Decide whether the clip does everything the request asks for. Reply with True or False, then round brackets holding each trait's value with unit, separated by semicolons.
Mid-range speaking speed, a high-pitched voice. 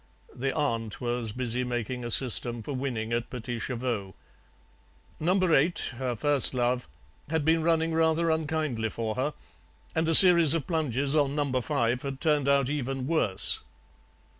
False (155 wpm; 135 Hz)